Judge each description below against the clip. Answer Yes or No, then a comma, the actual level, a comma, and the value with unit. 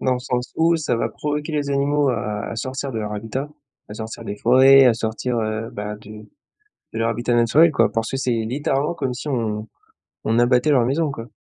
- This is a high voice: No, low, 125 Hz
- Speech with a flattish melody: No, average, 3.8 semitones